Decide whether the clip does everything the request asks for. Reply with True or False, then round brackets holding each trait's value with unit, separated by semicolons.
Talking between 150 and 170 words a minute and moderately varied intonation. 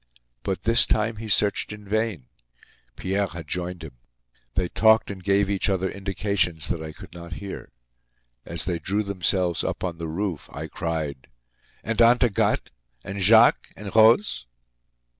True (160 wpm; 3.7 semitones)